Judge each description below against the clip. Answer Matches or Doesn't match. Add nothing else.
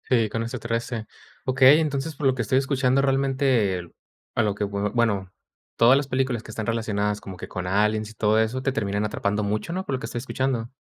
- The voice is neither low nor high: Doesn't match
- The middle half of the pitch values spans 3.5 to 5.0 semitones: Matches